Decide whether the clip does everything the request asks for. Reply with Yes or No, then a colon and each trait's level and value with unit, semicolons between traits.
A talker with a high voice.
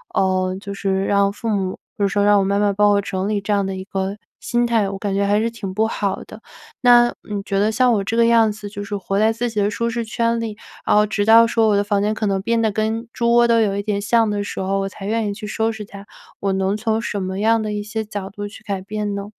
Yes: high, 205 Hz